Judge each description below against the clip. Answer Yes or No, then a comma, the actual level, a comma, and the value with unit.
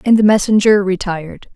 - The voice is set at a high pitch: Yes, high, 200 Hz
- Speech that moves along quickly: No, average, 155 wpm